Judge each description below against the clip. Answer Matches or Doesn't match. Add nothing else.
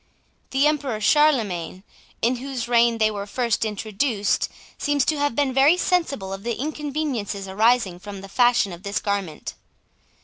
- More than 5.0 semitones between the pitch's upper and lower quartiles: Matches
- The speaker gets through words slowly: Doesn't match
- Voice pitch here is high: Matches